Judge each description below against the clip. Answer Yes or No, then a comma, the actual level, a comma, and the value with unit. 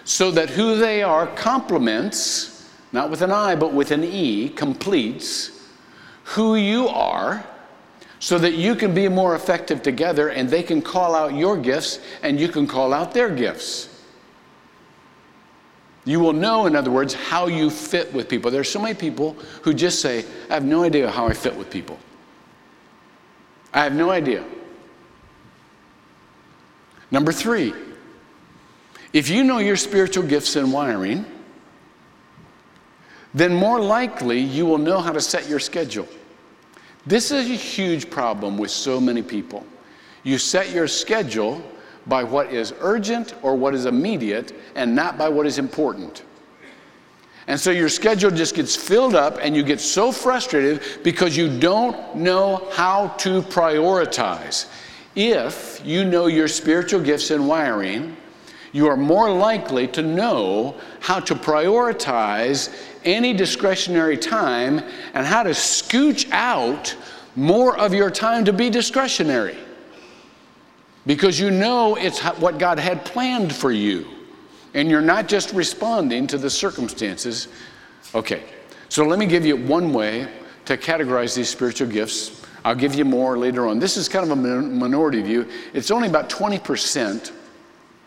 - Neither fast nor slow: Yes, average, 150 wpm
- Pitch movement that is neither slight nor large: No, wide, 6.0 semitones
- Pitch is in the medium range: Yes, medium, 170 Hz